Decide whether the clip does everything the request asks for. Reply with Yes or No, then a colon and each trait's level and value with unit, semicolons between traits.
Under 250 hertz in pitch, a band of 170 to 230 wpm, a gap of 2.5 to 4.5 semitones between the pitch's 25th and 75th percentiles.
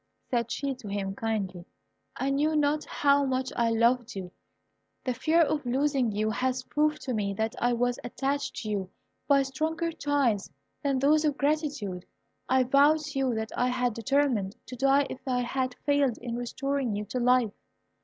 No: very high, 255 Hz; average, 180 wpm; average, 3.5 semitones